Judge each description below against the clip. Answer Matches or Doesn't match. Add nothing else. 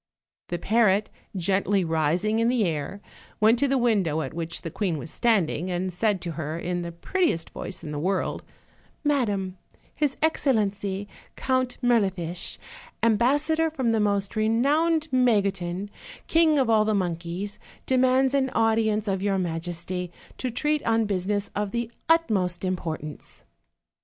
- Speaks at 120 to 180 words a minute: Matches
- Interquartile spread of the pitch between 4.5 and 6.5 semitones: Matches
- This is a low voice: Doesn't match